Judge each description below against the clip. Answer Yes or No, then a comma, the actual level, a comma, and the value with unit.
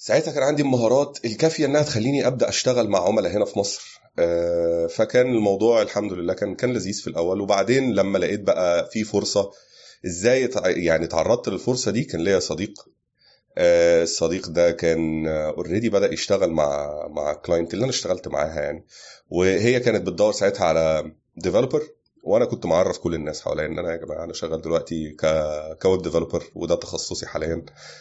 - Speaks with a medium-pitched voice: No, very low, 95 Hz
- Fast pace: Yes, fast, 160 wpm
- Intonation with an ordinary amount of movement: No, wide, 6.7 semitones